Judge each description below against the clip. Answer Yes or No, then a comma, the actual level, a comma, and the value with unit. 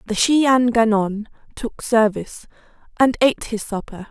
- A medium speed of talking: Yes, average, 145 wpm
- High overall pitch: Yes, high, 225 Hz